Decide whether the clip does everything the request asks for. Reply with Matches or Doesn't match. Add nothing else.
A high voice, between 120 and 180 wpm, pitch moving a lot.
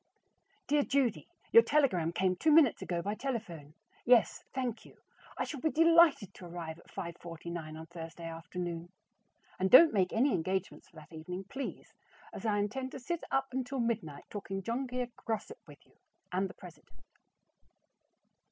Matches